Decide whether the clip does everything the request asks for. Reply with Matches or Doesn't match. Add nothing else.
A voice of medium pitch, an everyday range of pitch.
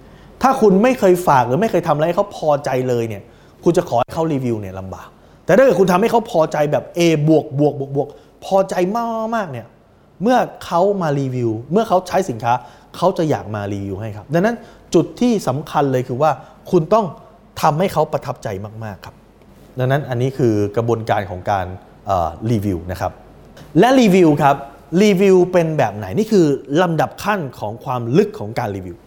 Doesn't match